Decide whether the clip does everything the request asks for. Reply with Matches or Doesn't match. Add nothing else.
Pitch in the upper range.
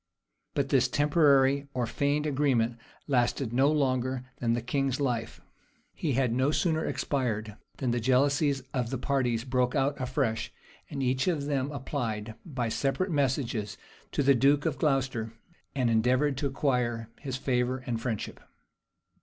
Doesn't match